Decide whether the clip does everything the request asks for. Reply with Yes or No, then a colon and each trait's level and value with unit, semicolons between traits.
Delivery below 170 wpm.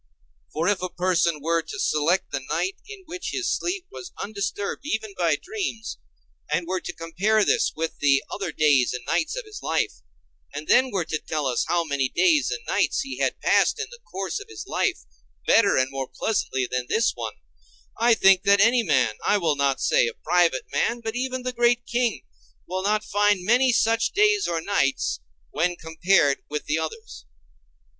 No: average, 190 wpm